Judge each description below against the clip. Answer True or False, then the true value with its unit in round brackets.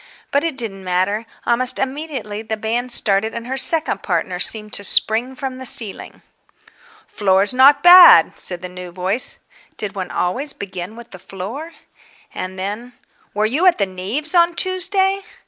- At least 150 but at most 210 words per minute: True (165 wpm)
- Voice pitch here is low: False (225 Hz)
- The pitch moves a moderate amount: False (6.2 semitones)